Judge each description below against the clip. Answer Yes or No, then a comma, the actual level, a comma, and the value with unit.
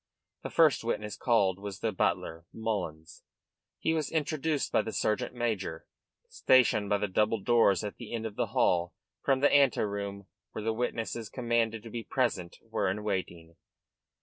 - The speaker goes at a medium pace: Yes, average, 170 wpm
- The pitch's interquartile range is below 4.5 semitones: Yes, average, 3.3 semitones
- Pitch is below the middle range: Yes, low, 110 Hz